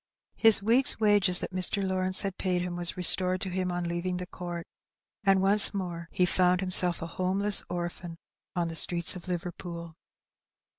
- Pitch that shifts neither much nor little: No, narrow, 1.6 semitones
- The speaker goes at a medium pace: Yes, average, 170 wpm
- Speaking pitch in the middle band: Yes, medium, 180 Hz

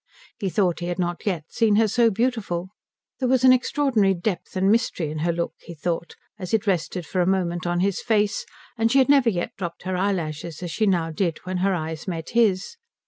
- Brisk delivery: Yes, fast, 220 wpm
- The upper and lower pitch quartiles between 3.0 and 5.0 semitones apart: Yes, average, 4.2 semitones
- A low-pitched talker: No, medium, 185 Hz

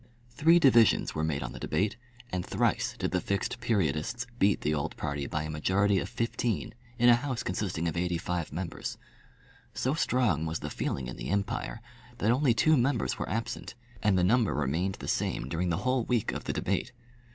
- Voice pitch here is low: Yes, low, 100 Hz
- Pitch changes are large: Yes, wide, 6.4 semitones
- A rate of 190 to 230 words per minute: Yes, average, 195 wpm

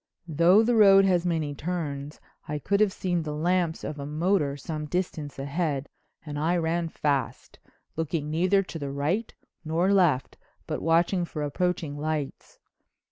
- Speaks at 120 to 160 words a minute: Yes, average, 155 wpm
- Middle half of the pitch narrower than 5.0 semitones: Yes, average, 3.5 semitones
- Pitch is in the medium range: Yes, medium, 160 Hz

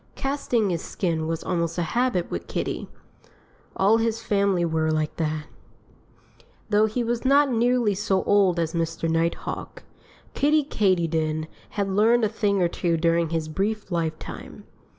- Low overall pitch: No, high, 190 Hz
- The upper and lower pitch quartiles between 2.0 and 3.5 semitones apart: No, average, 5.0 semitones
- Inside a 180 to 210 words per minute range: No, average, 150 wpm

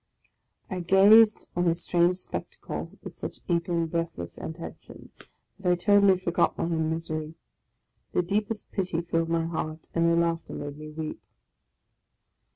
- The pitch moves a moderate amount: No, narrow, 1.9 semitones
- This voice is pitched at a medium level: Yes, medium, 170 Hz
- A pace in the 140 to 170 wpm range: Yes, average, 150 wpm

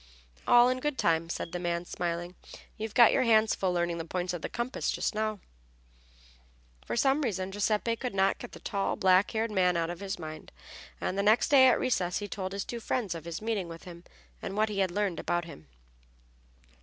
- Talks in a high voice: Yes, high, 195 Hz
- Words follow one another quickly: Yes, fast, 215 wpm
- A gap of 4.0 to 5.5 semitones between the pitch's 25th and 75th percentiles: Yes, average, 4.3 semitones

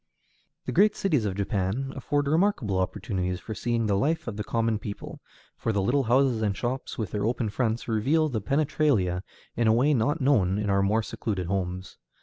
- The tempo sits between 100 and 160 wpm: No, average, 190 wpm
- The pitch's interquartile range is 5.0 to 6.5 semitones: Yes, average, 5.3 semitones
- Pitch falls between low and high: No, low, 110 Hz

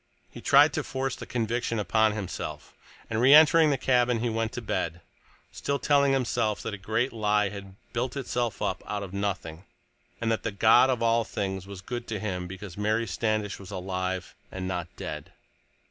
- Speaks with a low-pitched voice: Yes, low, 110 Hz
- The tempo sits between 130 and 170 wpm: No, average, 185 wpm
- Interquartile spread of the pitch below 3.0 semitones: No, average, 3.7 semitones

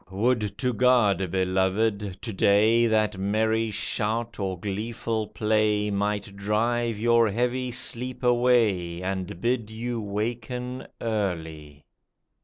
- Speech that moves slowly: Yes, slow, 110 wpm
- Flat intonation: No, average, 3.0 semitones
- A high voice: No, low, 110 Hz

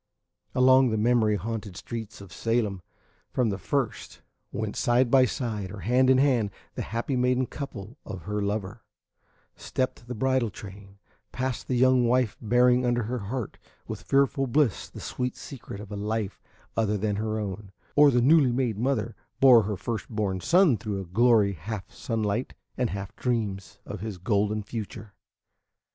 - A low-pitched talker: Yes, low, 115 Hz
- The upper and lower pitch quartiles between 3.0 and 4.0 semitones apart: Yes, average, 3.6 semitones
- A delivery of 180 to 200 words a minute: No, average, 165 wpm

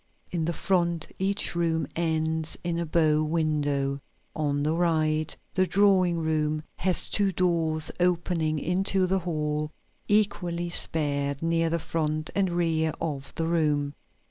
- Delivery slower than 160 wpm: Yes, average, 140 wpm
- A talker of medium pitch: Yes, medium, 165 Hz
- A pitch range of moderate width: No, narrow, 2.1 semitones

